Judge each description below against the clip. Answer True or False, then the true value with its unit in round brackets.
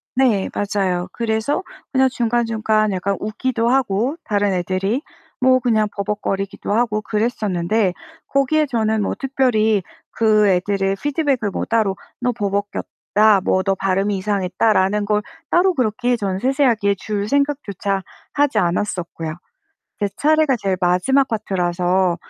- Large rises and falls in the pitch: False (4.0 semitones)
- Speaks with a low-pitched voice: False (210 Hz)